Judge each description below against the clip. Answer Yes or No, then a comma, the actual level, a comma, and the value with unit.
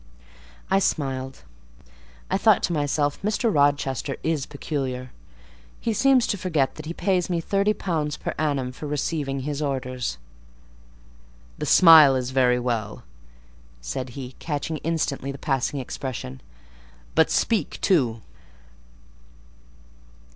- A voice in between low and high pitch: Yes, medium, 145 Hz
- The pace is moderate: No, slow, 115 wpm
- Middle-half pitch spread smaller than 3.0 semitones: No, average, 4.1 semitones